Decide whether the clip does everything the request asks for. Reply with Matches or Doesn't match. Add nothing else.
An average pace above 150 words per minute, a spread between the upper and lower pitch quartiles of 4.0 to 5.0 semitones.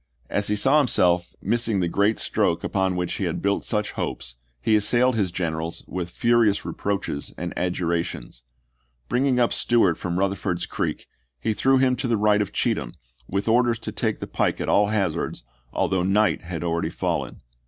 Matches